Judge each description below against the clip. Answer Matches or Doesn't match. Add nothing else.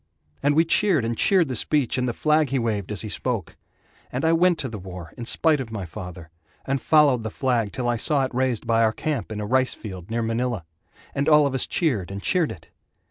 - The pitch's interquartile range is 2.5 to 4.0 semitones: Doesn't match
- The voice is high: Doesn't match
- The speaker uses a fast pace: Matches